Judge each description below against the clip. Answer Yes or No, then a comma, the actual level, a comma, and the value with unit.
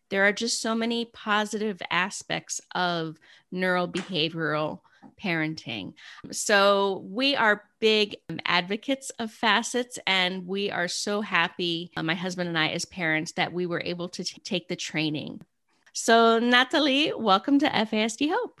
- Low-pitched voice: No, high, 195 Hz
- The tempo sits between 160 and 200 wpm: No, average, 145 wpm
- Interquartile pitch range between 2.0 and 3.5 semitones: No, average, 4.5 semitones